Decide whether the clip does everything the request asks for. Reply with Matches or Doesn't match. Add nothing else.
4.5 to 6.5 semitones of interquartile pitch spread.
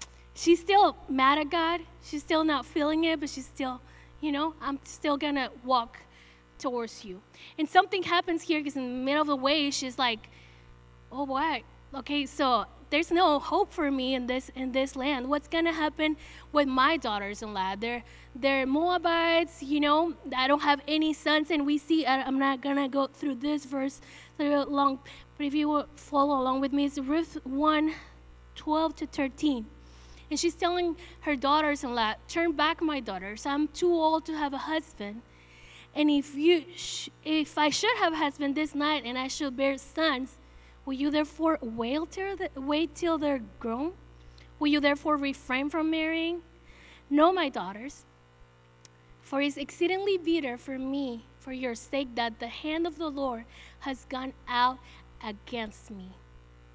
Doesn't match